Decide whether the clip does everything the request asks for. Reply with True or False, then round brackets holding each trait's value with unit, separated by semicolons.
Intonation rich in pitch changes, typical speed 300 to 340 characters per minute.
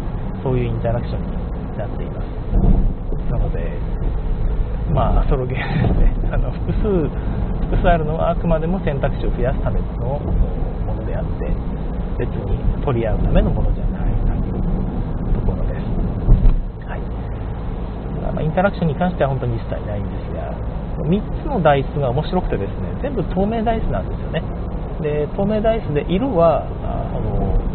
True (5.9 semitones; 335 characters per minute)